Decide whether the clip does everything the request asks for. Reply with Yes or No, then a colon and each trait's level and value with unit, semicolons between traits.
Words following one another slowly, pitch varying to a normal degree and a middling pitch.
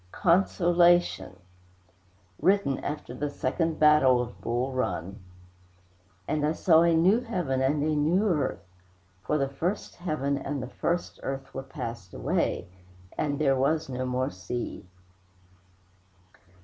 Yes: slow, 130 wpm; average, 4.5 semitones; medium, 145 Hz